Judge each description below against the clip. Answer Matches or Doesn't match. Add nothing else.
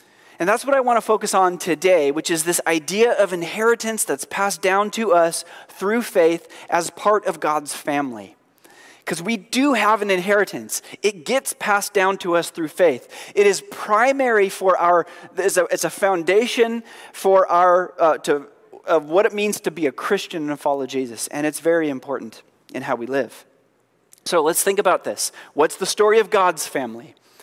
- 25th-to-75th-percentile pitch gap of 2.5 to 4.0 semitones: Doesn't match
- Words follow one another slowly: Doesn't match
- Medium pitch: Doesn't match